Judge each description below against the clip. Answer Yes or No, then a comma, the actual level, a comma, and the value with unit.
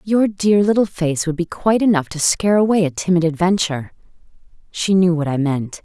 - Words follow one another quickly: No, average, 195 wpm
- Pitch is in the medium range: Yes, medium, 175 Hz